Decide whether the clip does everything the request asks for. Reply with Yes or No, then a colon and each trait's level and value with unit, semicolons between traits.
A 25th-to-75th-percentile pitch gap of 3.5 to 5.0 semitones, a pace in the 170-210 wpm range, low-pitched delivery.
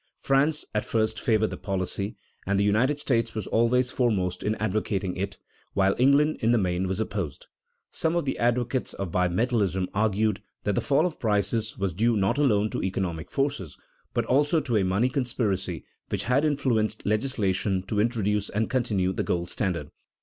Yes: average, 4.4 semitones; average, 175 wpm; low, 110 Hz